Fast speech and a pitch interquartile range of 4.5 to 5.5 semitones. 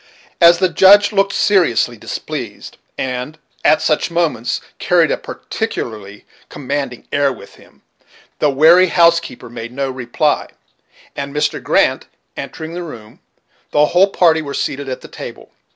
No: average, 140 wpm; average, 5.1 semitones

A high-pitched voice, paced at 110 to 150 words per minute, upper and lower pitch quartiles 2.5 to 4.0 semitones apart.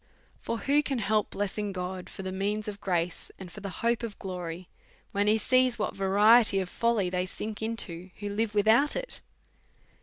No: high, 205 Hz; average, 185 wpm; average, 3.0 semitones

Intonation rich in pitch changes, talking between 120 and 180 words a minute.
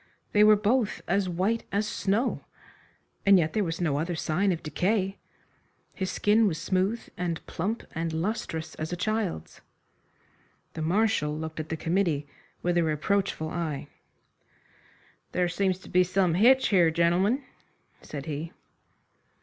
No: average, 4.0 semitones; average, 145 wpm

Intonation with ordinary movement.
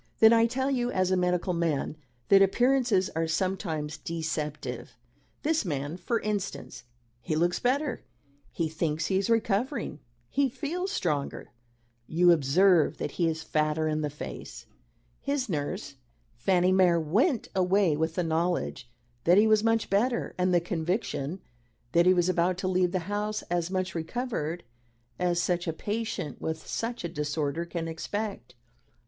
Yes: average, 4.8 semitones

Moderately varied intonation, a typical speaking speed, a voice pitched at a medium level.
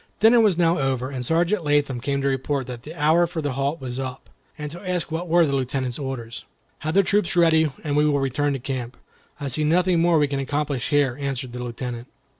No: average, 3.7 semitones; fast, 230 wpm; medium, 145 Hz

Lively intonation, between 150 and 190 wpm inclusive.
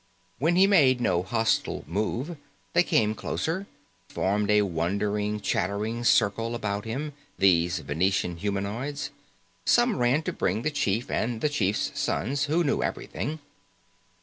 No: wide, 6.2 semitones; average, 140 wpm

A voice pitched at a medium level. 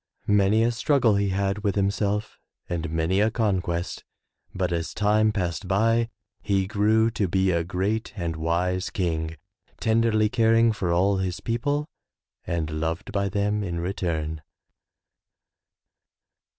No: low, 100 Hz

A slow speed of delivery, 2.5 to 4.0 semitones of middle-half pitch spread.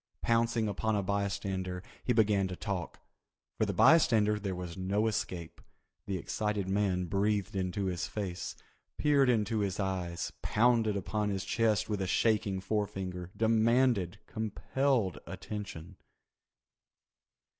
Yes: slow, 125 wpm; average, 2.8 semitones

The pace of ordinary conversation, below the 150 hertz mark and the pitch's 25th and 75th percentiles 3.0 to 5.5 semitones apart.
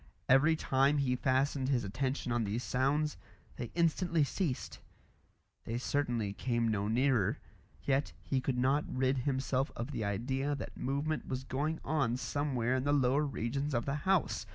No: average, 160 wpm; low, 135 Hz; narrow, 2.6 semitones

